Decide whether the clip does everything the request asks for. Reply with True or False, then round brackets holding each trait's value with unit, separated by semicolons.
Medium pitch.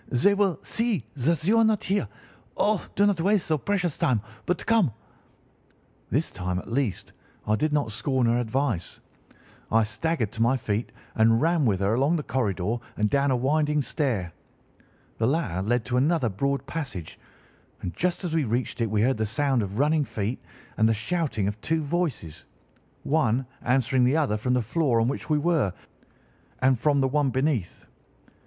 False (130 Hz)